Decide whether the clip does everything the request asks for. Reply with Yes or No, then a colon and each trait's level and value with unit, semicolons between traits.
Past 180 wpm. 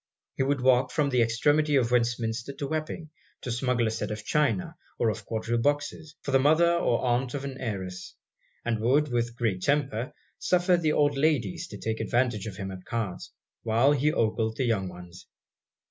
Yes: average, 190 wpm